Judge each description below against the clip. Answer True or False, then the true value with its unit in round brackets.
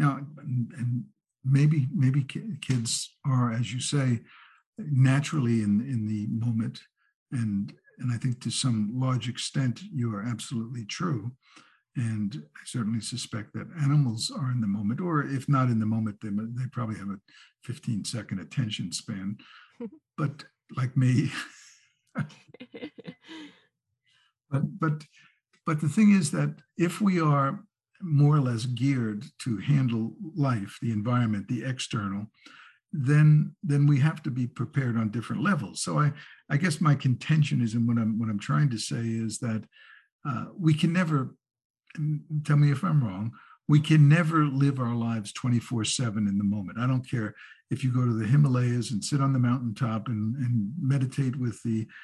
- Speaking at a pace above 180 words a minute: False (165 wpm)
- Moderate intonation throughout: True (4.3 semitones)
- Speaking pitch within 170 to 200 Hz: False (130 Hz)